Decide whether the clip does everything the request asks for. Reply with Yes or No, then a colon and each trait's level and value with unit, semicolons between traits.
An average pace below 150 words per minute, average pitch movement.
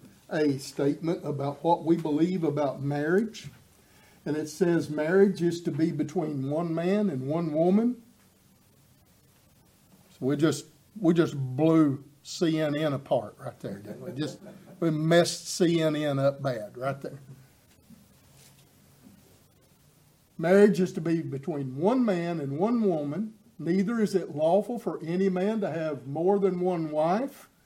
Yes: average, 140 wpm; average, 4.1 semitones